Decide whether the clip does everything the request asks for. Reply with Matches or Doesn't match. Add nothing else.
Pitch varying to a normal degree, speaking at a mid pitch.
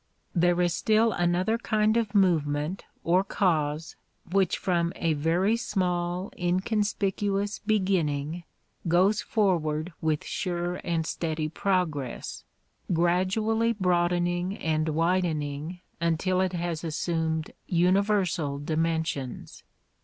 Matches